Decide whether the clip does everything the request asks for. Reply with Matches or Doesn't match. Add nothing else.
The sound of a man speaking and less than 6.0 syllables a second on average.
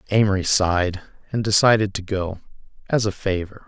Matches